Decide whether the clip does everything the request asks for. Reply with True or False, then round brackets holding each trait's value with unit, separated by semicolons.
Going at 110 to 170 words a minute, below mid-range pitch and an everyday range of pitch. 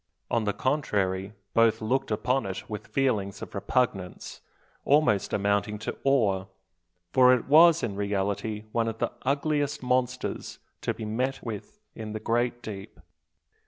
True (145 wpm; 115 Hz; 4.0 semitones)